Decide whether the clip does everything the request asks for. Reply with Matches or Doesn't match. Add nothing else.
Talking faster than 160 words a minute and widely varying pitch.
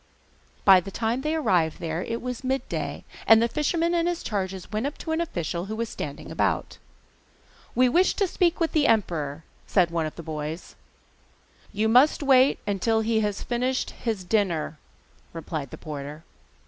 Matches